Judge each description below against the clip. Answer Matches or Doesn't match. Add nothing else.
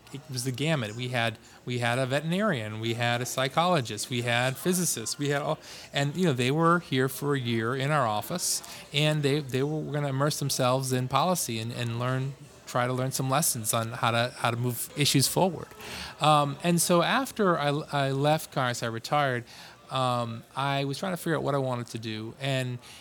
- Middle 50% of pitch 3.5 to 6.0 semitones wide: Matches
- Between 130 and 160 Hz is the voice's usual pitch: Matches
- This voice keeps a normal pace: Doesn't match